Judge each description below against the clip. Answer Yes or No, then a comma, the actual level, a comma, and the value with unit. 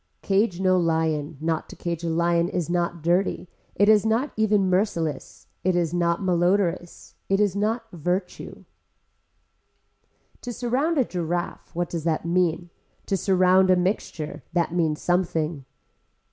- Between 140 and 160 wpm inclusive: Yes, average, 145 wpm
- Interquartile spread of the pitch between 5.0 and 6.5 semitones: No, narrow, 2.5 semitones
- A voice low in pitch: No, medium, 175 Hz